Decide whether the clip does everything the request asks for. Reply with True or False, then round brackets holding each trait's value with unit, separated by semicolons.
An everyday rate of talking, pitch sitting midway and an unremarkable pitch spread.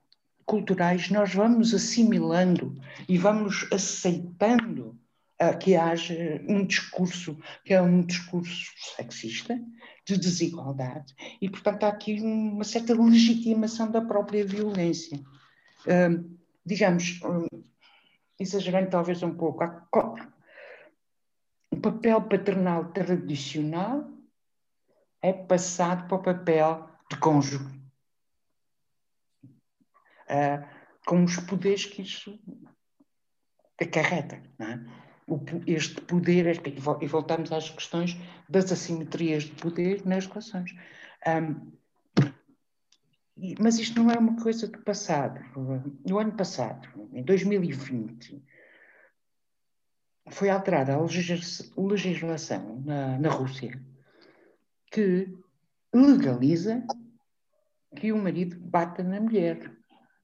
False (95 wpm; 180 Hz; 4.3 semitones)